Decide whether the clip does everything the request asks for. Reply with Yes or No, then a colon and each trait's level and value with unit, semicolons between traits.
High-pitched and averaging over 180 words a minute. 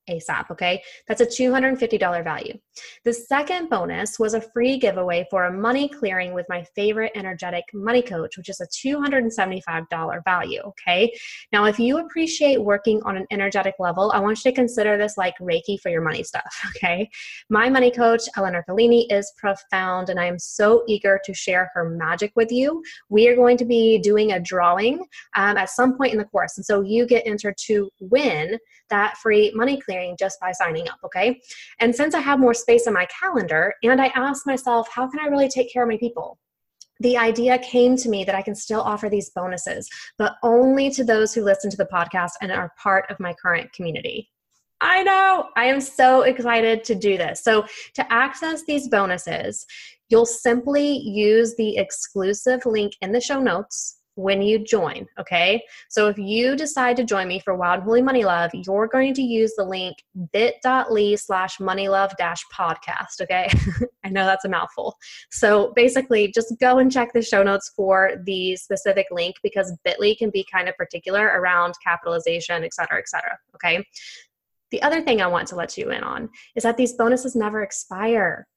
Yes: high, 210 Hz; average, 190 wpm